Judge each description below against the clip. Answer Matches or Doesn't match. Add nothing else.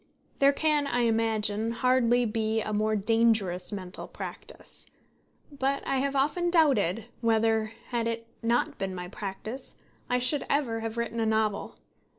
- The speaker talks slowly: Doesn't match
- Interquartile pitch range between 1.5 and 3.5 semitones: Matches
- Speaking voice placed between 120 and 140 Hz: Doesn't match